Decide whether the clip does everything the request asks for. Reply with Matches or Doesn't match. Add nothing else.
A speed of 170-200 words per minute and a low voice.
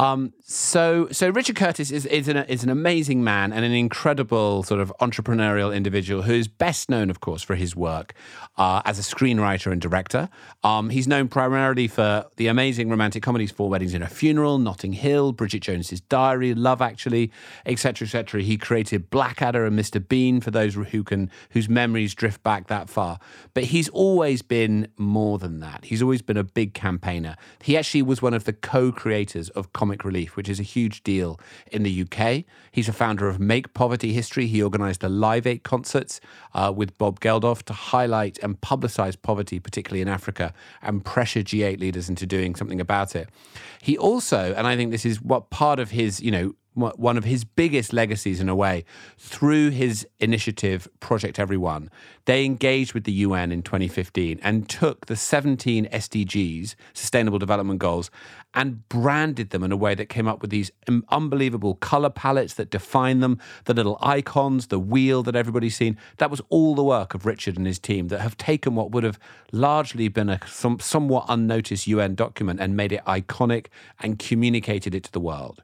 Matches